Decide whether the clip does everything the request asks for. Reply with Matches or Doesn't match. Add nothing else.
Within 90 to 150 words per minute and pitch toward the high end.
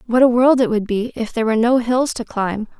Doesn't match